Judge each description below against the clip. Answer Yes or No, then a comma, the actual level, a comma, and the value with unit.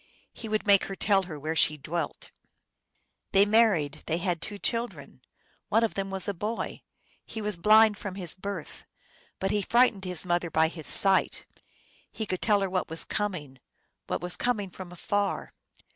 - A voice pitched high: Yes, high, 195 Hz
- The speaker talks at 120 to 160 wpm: No, average, 175 wpm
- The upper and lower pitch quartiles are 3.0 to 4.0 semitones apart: Yes, average, 3.4 semitones